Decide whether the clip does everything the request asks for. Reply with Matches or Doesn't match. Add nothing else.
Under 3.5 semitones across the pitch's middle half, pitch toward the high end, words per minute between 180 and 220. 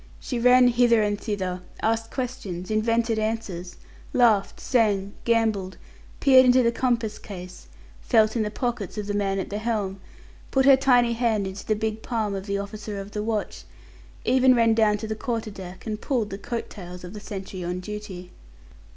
Matches